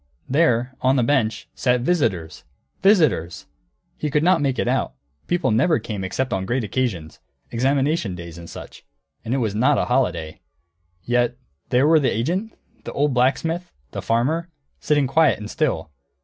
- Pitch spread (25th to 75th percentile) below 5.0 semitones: No, wide, 5.5 semitones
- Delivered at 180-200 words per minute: No, average, 165 wpm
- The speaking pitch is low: Yes, low, 130 Hz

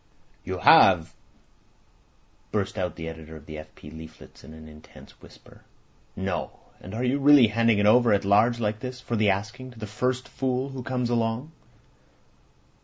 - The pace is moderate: Yes, average, 175 wpm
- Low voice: Yes, low, 110 Hz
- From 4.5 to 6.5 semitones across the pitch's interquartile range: Yes, wide, 5.4 semitones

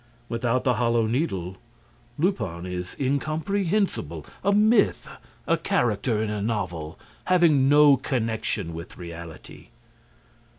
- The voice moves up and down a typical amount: No, wide, 8.6 semitones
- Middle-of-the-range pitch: No, low, 115 Hz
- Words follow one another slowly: Yes, slow, 110 wpm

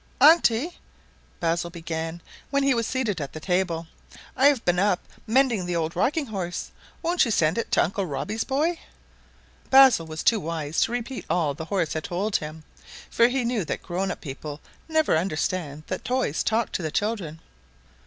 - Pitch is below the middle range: No, high, 190 Hz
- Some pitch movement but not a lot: No, wide, 6.9 semitones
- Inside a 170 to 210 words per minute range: Yes, average, 185 wpm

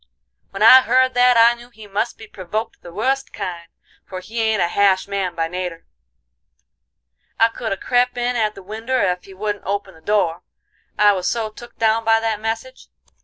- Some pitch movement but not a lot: Yes, average, 3.4 semitones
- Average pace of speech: Yes, average, 195 wpm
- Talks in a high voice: Yes, high, 215 Hz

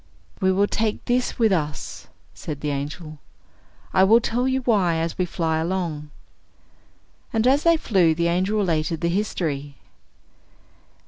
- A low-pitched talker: No, medium, 180 Hz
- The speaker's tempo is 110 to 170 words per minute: Yes, average, 145 wpm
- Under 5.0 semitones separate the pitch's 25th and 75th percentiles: No, average, 5.3 semitones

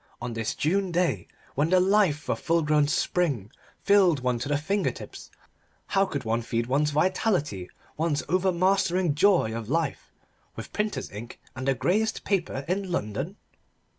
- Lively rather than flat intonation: Yes, wide, 6.3 semitones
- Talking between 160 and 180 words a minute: Yes, average, 165 wpm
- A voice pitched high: No, medium, 155 Hz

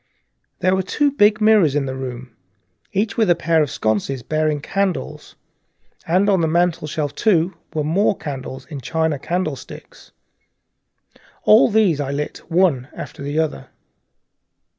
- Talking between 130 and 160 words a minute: Yes, average, 140 wpm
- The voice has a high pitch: No, medium, 160 Hz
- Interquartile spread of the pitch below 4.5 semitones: No, average, 5.1 semitones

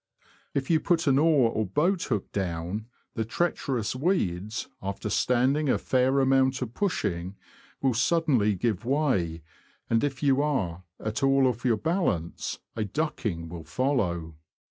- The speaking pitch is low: Yes, low, 125 Hz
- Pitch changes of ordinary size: No, wide, 6.1 semitones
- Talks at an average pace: Yes, average, 145 wpm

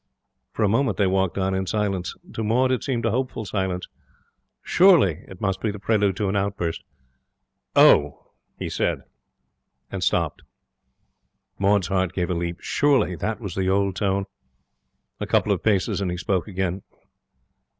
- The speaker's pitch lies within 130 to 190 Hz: No, very low, 95 Hz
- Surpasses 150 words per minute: Yes, average, 160 wpm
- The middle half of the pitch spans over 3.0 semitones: No, narrow, 2.6 semitones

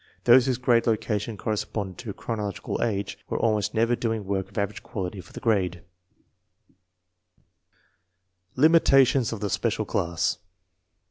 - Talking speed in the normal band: No, slow, 130 wpm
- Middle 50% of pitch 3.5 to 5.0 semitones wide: No, average, 3.0 semitones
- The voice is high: No, low, 110 Hz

